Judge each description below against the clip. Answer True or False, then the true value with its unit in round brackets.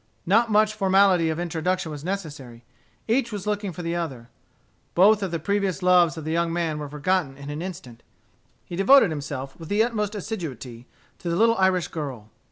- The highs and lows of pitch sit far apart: False (4.8 semitones)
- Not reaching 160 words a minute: False (185 wpm)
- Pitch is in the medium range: True (175 Hz)